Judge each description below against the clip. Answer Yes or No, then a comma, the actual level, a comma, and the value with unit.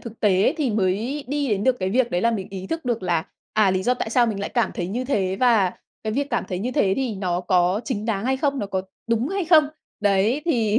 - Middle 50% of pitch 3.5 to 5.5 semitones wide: Yes, average, 5.0 semitones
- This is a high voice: Yes, high, 220 Hz